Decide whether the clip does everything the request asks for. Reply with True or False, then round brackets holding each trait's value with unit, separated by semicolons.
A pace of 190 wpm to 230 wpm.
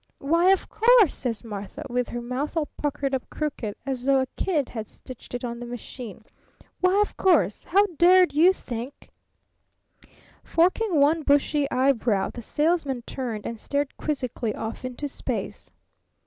False (160 wpm)